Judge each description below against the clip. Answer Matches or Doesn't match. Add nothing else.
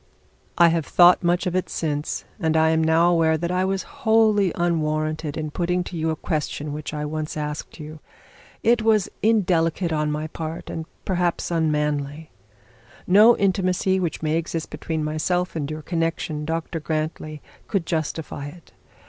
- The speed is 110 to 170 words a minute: Matches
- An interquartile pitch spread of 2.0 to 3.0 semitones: Matches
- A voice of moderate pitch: Matches